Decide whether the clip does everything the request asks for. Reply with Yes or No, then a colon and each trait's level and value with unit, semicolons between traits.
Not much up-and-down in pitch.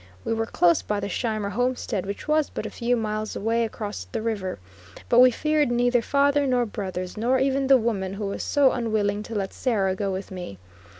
No: average, 3.8 semitones